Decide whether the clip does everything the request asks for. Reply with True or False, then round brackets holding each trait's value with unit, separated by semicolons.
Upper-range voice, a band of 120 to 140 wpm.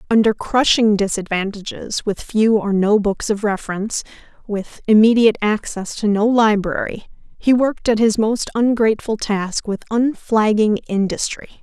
True (215 Hz; 135 wpm)